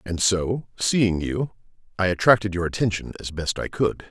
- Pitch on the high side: No, low, 100 Hz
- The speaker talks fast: No, average, 175 wpm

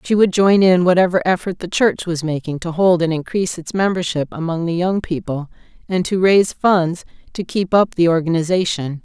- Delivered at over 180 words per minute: Yes, average, 190 wpm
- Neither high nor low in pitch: Yes, medium, 175 Hz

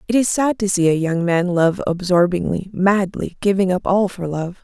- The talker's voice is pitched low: No, medium, 185 Hz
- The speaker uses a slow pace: No, fast, 205 wpm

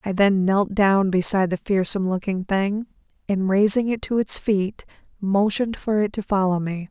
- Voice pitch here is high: Yes, high, 195 Hz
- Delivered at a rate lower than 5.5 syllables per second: Yes, 5.0 syllables/s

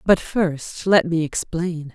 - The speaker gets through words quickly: No, average, 155 wpm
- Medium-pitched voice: Yes, medium, 170 Hz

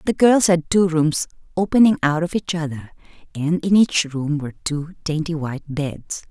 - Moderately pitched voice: Yes, medium, 165 Hz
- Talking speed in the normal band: Yes, average, 180 wpm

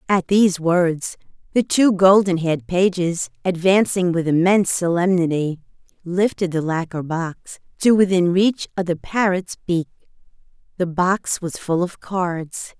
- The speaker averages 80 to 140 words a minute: Yes, slow, 135 wpm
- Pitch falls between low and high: Yes, medium, 180 Hz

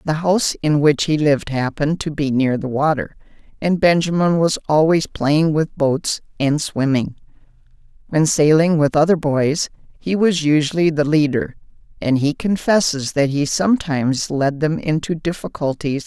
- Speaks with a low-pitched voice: No, medium, 155 Hz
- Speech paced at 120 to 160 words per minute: Yes, average, 155 wpm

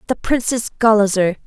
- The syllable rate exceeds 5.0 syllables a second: Yes, 5.2 syllables/s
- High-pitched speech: Yes, high, 220 Hz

